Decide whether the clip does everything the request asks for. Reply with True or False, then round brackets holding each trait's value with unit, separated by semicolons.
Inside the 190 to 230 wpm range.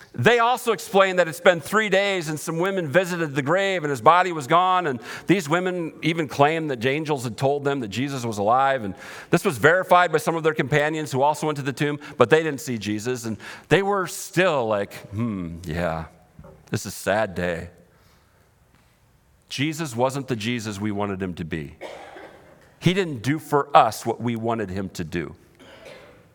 True (195 wpm)